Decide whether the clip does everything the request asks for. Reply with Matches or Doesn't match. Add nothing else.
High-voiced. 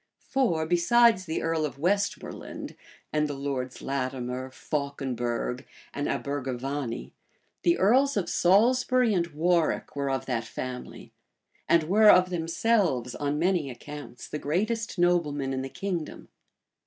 Doesn't match